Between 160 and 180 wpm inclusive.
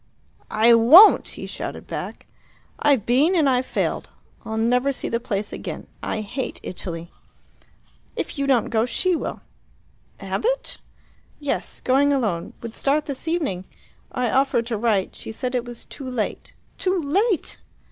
No: average, 150 wpm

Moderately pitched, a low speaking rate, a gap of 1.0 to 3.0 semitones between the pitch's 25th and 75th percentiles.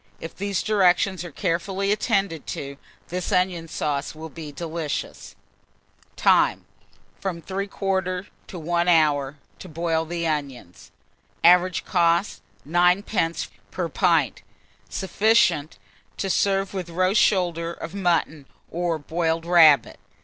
Yes: medium, 175 Hz; slow, 120 wpm; average, 2.7 semitones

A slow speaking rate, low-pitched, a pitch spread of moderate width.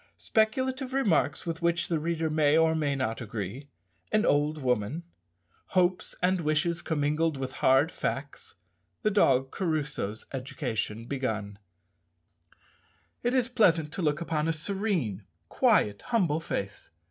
No: slow, 130 wpm; medium, 155 Hz; average, 5.0 semitones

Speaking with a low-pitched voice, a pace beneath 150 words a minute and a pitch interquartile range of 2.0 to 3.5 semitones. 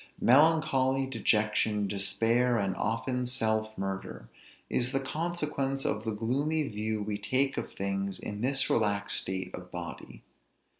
No: low, 110 Hz; slow, 135 wpm; average, 4.7 semitones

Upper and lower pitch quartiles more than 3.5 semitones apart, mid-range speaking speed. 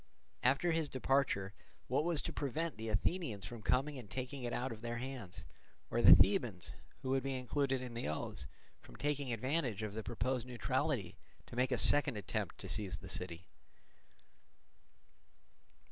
Yes: average, 4.1 semitones; average, 165 wpm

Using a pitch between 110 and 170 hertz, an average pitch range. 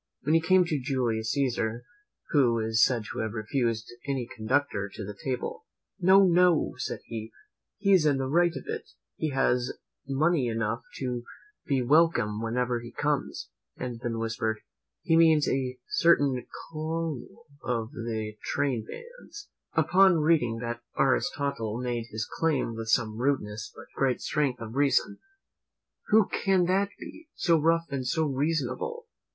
No: low, 135 Hz; wide, 5.9 semitones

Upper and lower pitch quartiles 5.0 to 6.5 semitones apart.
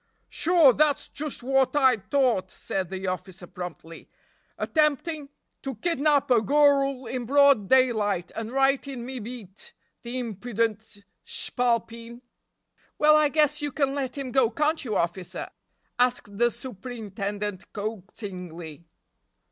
Yes: average, 5.3 semitones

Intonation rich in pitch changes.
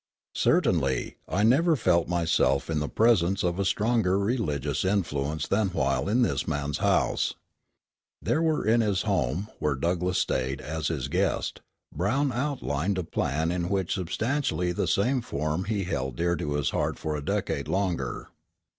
Yes: wide, 5.8 semitones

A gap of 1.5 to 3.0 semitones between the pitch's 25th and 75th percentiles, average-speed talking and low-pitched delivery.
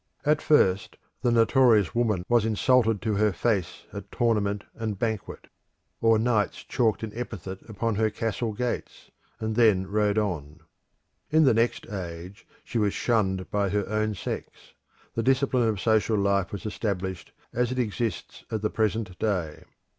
Yes: narrow, 2.6 semitones; average, 155 wpm; low, 110 Hz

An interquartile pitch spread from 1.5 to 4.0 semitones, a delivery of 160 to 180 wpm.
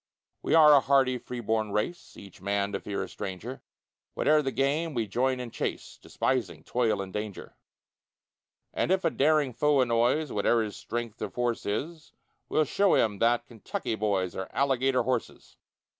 No: average, 4.6 semitones; average, 170 wpm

